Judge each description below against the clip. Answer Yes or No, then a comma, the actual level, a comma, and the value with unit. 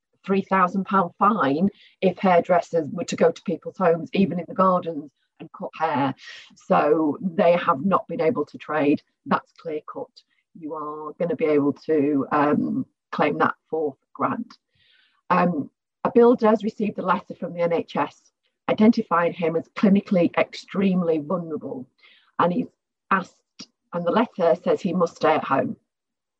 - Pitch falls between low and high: Yes, medium, 180 Hz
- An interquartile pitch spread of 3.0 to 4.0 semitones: Yes, average, 3.6 semitones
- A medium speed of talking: Yes, average, 155 wpm